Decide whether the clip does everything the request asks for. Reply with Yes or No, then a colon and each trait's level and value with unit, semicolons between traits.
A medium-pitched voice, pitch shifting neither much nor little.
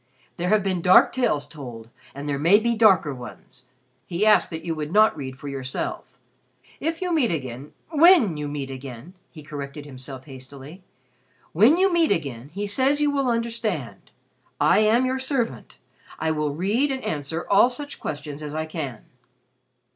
No: medium, 165 Hz; wide, 8.6 semitones